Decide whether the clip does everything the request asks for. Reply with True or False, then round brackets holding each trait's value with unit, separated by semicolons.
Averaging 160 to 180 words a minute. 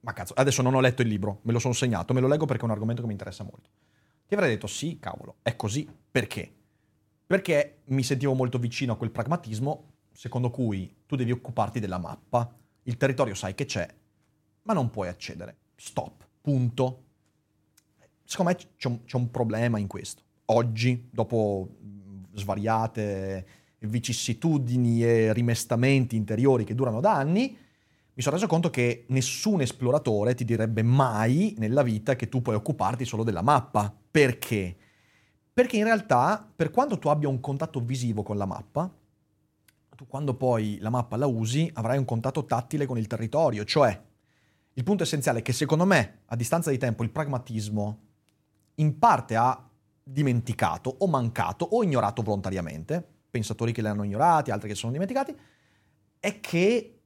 True (165 wpm)